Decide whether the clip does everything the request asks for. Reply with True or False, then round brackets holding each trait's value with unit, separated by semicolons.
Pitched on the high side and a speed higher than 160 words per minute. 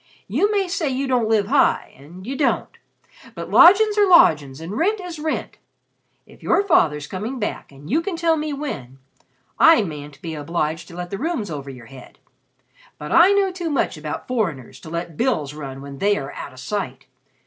True (210 Hz; 195 wpm)